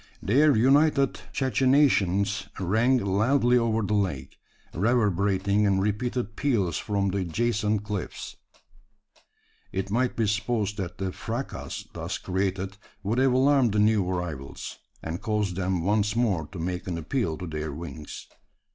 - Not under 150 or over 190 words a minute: No, average, 140 wpm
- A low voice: Yes, low, 105 Hz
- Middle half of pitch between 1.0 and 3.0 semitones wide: No, average, 4.1 semitones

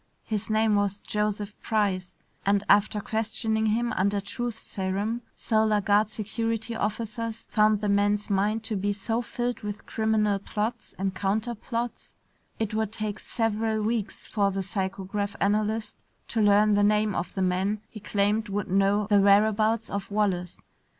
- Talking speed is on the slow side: No, average, 155 wpm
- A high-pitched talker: Yes, high, 210 Hz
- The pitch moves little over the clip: Yes, narrow, 1.6 semitones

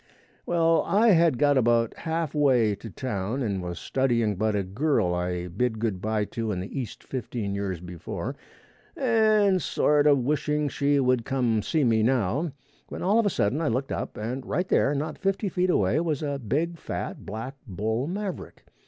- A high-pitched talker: No, low, 130 Hz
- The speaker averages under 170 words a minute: No, average, 185 wpm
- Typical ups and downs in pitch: No, wide, 6.5 semitones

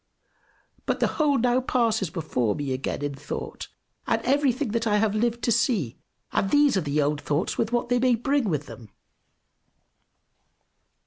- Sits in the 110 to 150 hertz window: No, high, 220 Hz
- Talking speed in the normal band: Yes, average, 170 wpm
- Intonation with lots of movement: Yes, wide, 8.9 semitones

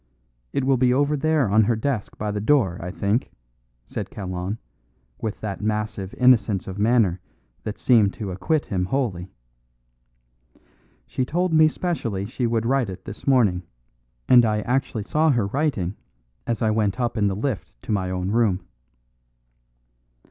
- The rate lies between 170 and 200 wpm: No, average, 160 wpm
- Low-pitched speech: Yes, low, 110 Hz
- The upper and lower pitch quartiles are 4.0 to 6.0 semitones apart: Yes, average, 4.6 semitones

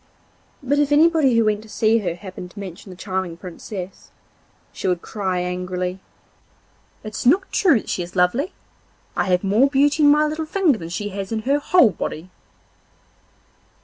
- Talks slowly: No, average, 175 wpm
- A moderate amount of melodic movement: No, wide, 7.8 semitones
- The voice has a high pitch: Yes, high, 210 Hz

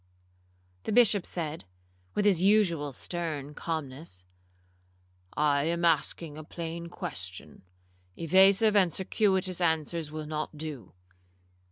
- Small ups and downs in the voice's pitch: No, average, 3.8 semitones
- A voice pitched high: No, medium, 160 Hz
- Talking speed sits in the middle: No, slow, 100 wpm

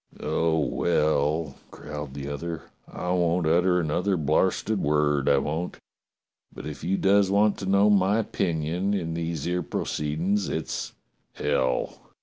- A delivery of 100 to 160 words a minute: Yes, average, 140 wpm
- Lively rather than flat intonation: No, average, 4.0 semitones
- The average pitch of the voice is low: Yes, very low, 85 Hz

